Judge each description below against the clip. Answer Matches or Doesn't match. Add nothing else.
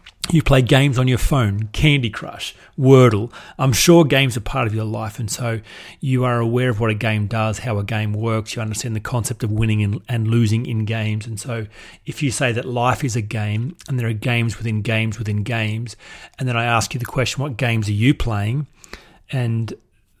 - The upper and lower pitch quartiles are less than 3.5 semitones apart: Matches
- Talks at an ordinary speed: Doesn't match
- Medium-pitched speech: Doesn't match